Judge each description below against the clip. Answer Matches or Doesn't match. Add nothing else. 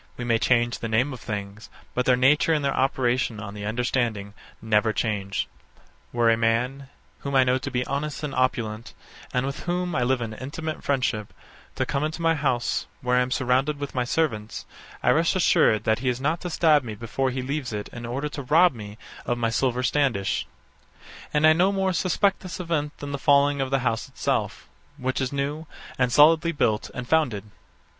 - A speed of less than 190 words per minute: Doesn't match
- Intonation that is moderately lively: Matches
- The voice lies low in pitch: Matches